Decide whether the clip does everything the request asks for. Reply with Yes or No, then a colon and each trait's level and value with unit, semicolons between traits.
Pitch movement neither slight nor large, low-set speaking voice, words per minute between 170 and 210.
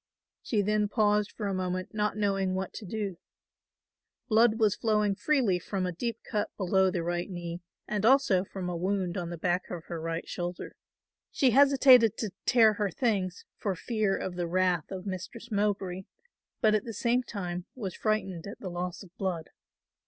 No: average, 3.1 semitones; high, 195 Hz; average, 180 wpm